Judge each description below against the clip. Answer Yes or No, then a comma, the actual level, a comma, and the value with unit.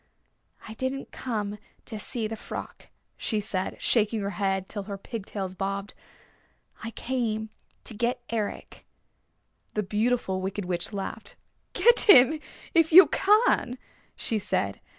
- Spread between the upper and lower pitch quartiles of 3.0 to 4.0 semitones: Yes, average, 3.6 semitones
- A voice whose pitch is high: Yes, high, 215 Hz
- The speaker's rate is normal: No, slow, 130 wpm